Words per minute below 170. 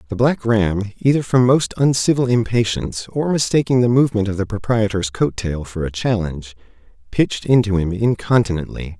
Yes: average, 160 wpm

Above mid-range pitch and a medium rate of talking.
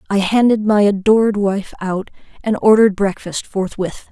Yes: high, 205 Hz; average, 145 wpm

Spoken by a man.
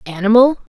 No: female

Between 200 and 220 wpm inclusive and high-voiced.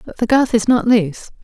No: fast, 250 wpm; high, 230 Hz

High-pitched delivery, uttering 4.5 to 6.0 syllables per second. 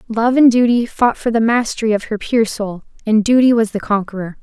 Yes: high, 225 Hz; 5.5 syllables/s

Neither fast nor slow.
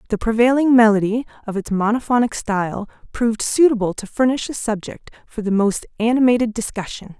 Yes: average, 150 wpm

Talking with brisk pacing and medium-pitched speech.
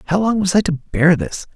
Yes: fast, 270 wpm; medium, 175 Hz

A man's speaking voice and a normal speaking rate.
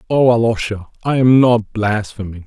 Yes: male; average, 145 wpm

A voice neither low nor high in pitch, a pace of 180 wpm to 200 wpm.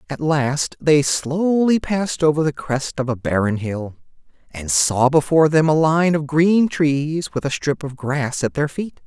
Yes: medium, 145 Hz; average, 190 wpm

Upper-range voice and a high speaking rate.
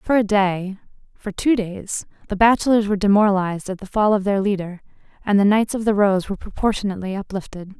No: high, 200 Hz; average, 175 wpm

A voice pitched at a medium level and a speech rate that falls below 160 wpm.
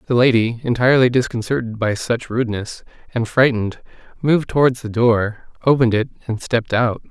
No: low, 120 Hz; average, 150 wpm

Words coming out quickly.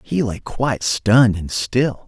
No: average, 175 wpm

